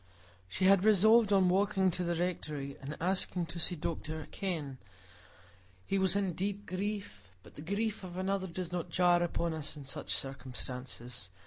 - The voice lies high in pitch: No, medium, 180 Hz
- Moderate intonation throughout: Yes, average, 4.2 semitones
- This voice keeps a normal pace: Yes, average, 165 wpm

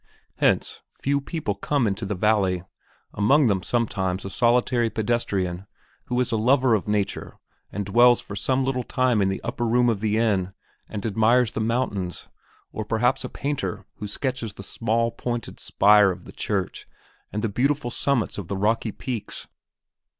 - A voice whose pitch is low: Yes, low, 110 Hz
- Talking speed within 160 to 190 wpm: Yes, average, 170 wpm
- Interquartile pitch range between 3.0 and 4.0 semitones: Yes, average, 3.5 semitones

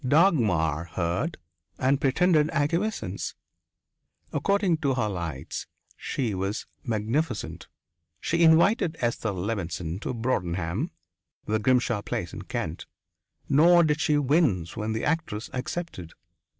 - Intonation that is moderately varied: No, wide, 8.5 semitones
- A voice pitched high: No, low, 125 Hz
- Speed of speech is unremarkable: No, slow, 110 wpm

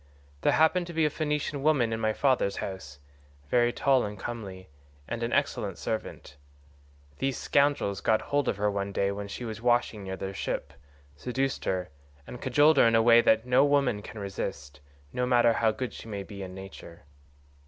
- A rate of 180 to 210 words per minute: Yes, average, 185 wpm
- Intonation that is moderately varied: Yes, average, 5.0 semitones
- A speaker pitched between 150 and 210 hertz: No, low, 115 Hz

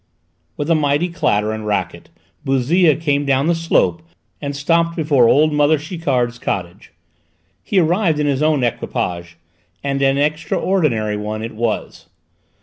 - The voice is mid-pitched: Yes, medium, 145 Hz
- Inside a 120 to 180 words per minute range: Yes, average, 145 wpm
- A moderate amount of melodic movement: Yes, average, 5.0 semitones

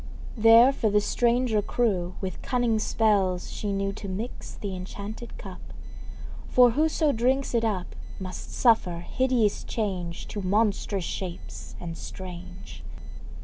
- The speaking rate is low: Yes, slow, 130 wpm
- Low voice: No, high, 210 Hz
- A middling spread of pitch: Yes, average, 4.2 semitones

